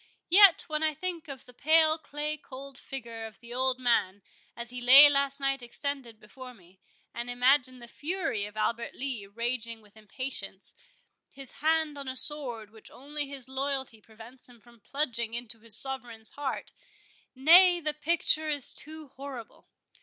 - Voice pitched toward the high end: Yes, very high, 260 Hz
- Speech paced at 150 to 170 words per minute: Yes, average, 160 wpm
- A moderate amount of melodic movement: Yes, average, 3.9 semitones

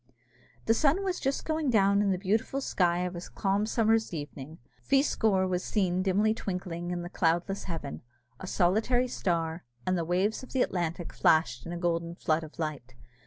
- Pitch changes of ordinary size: Yes, average, 4.3 semitones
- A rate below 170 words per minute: No, average, 180 wpm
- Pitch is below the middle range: No, medium, 185 Hz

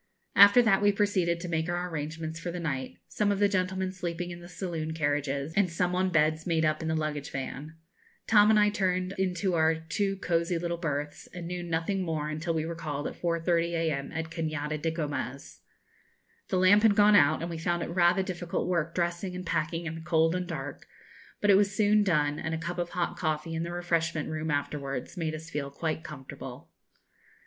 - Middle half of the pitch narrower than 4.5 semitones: Yes, narrow, 2.5 semitones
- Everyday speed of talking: No, fast, 210 wpm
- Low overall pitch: No, medium, 170 Hz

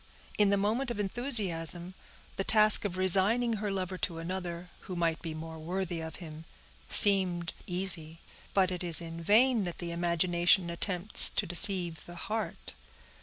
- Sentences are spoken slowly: No, average, 160 wpm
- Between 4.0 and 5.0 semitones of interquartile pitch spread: No, average, 2.9 semitones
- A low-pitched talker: No, medium, 180 Hz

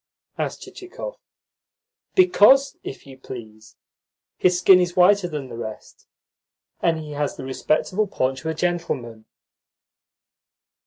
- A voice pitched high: No, medium, 160 Hz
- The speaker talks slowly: Yes, slow, 120 wpm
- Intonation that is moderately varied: No, wide, 5.8 semitones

